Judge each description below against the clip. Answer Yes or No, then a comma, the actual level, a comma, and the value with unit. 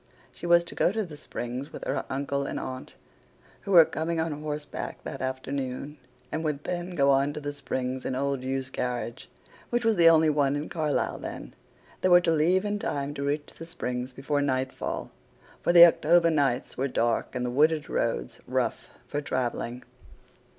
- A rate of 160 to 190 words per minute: Yes, average, 185 wpm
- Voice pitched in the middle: Yes, medium, 145 Hz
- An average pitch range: Yes, average, 3.9 semitones